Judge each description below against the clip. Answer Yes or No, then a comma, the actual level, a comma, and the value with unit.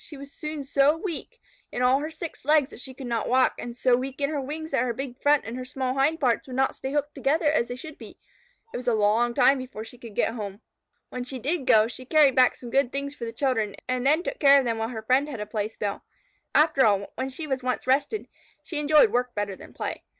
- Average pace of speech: No, fast, 260 wpm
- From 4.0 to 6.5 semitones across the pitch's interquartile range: No, average, 3.2 semitones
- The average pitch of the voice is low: No, very high, 260 Hz